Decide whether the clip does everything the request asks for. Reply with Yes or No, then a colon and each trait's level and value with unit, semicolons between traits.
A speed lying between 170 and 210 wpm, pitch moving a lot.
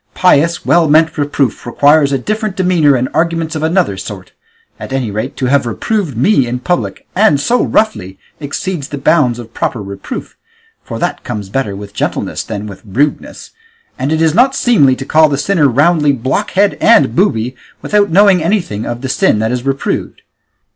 Yes: average, 180 wpm; wide, 6.1 semitones